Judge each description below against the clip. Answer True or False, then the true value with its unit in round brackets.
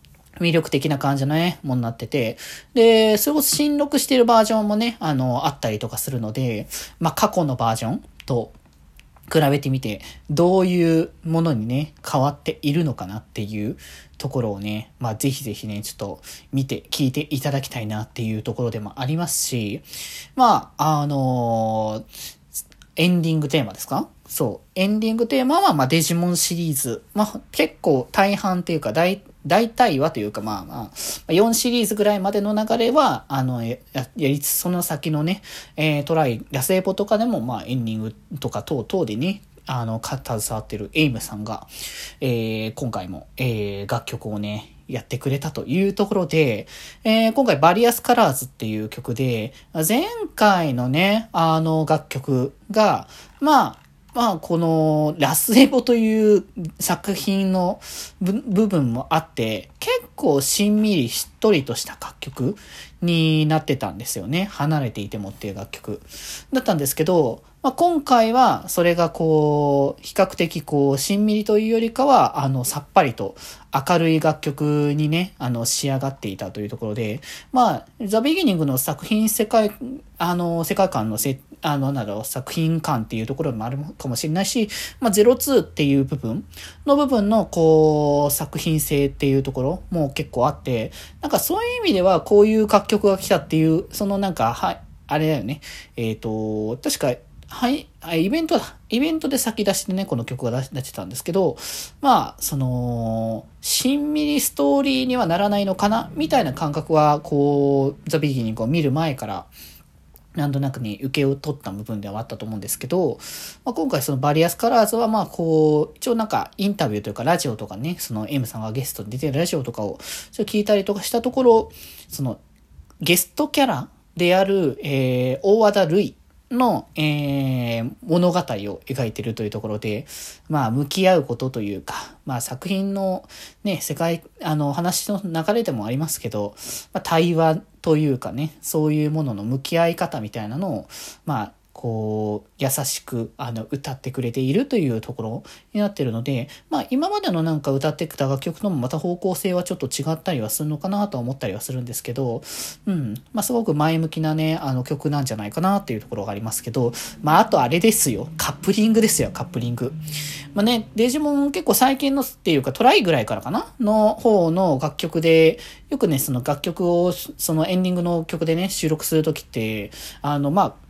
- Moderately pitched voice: True (155 Hz)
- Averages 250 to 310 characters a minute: False (360 characters per minute)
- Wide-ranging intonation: True (7.6 semitones)